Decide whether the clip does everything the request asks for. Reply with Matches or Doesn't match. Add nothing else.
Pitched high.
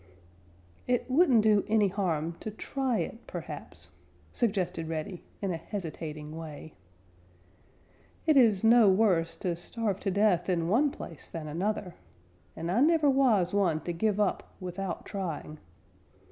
Matches